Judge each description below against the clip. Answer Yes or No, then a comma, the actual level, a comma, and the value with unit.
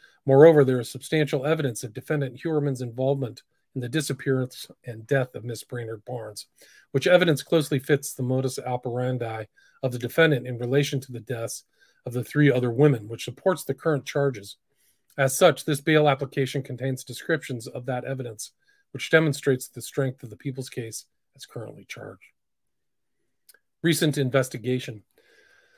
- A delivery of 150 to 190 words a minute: Yes, average, 155 wpm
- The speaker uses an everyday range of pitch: Yes, average, 3.0 semitones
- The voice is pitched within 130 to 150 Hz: Yes, low, 135 Hz